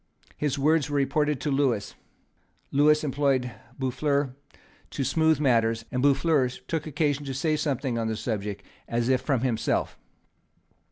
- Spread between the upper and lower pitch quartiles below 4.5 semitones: Yes, average, 3.1 semitones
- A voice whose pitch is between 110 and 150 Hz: Yes, low, 135 Hz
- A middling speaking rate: Yes, average, 145 wpm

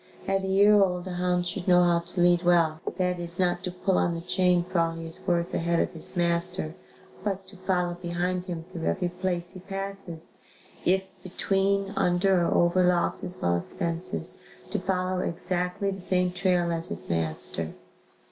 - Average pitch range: No, narrow, 1.4 semitones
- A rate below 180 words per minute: No, average, 190 wpm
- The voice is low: No, medium, 180 Hz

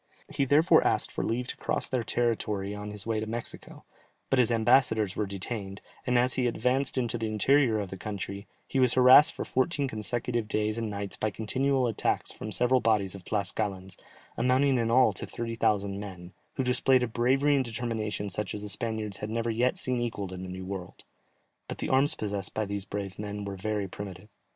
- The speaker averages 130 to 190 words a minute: No, average, 200 wpm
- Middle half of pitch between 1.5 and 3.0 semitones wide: No, average, 3.6 semitones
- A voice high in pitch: No, low, 110 Hz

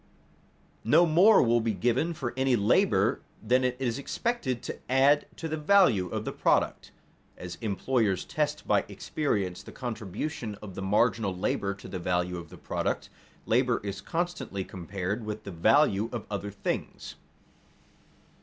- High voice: No, low, 115 Hz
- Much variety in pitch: Yes, wide, 6.1 semitones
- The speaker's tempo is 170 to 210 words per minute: No, average, 155 wpm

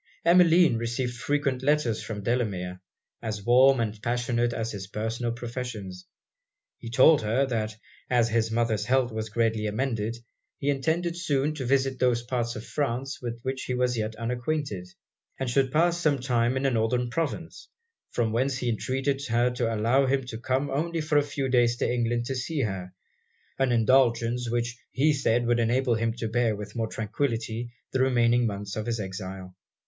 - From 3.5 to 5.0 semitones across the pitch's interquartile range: No, average, 2.9 semitones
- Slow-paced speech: No, average, 175 wpm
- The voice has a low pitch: Yes, low, 120 Hz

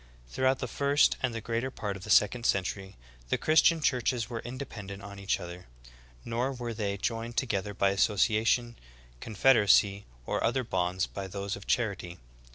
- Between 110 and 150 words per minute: No, average, 165 wpm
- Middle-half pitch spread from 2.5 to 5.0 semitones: Yes, average, 3.7 semitones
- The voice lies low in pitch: Yes, low, 110 Hz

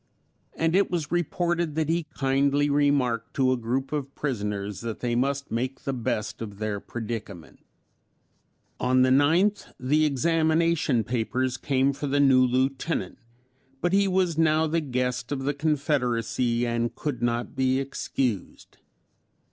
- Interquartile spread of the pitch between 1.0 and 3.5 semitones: No, average, 4.2 semitones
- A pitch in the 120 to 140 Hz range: Yes, low, 135 Hz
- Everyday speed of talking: Yes, average, 145 wpm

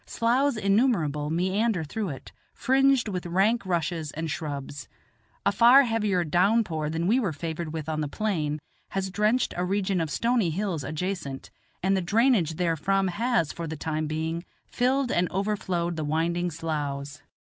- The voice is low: No, medium, 175 Hz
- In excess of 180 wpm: No, average, 160 wpm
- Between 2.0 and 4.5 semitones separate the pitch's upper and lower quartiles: No, average, 5.1 semitones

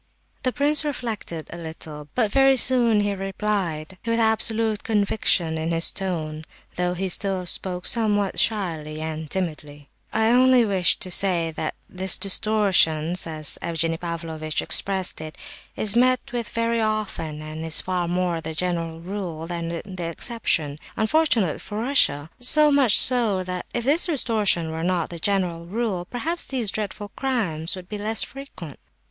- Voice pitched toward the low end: No, high, 190 Hz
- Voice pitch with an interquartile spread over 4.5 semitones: Yes, average, 5.3 semitones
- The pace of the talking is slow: No, average, 155 wpm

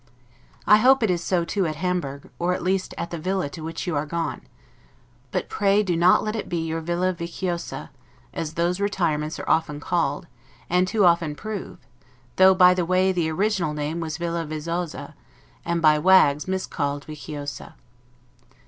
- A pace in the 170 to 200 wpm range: Yes, average, 175 wpm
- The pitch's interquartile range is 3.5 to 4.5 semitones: No, average, 2.9 semitones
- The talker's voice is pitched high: No, medium, 170 Hz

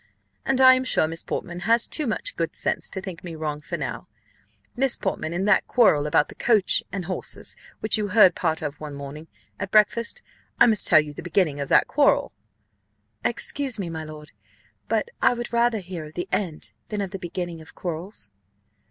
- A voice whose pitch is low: No, medium, 185 Hz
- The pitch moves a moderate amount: No, wide, 5.9 semitones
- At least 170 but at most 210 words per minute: Yes, average, 200 wpm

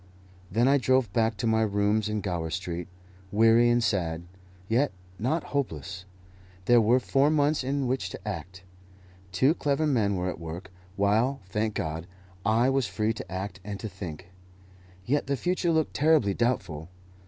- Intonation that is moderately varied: No, wide, 5.8 semitones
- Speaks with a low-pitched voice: Yes, low, 110 Hz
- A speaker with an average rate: Yes, average, 165 wpm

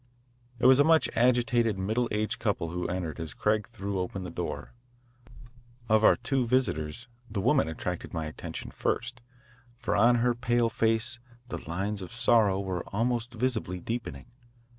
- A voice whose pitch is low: Yes, low, 110 Hz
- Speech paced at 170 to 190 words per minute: No, average, 160 wpm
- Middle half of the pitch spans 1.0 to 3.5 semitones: No, average, 4.1 semitones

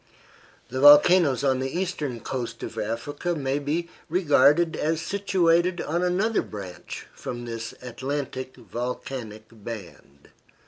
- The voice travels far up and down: Yes, wide, 6.0 semitones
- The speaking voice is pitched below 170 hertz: Yes, medium, 140 Hz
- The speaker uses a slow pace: Yes, slow, 120 wpm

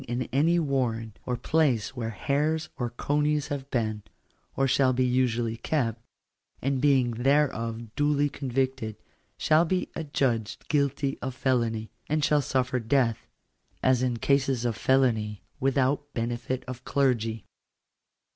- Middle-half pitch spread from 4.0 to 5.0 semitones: No, average, 3.3 semitones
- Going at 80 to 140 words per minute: Yes, slow, 135 wpm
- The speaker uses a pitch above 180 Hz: No, low, 130 Hz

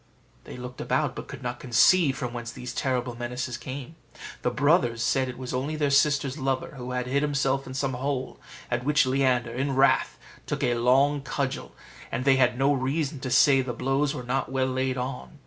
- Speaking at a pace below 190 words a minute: No, average, 200 wpm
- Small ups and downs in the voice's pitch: Yes, narrow, 1.9 semitones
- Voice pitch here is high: No, low, 130 Hz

